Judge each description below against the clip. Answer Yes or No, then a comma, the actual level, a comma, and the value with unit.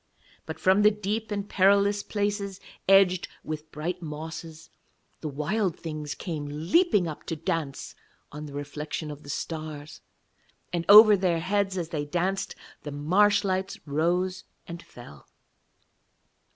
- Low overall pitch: No, medium, 170 Hz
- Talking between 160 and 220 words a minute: No, average, 140 wpm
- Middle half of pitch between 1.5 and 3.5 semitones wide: No, average, 4.5 semitones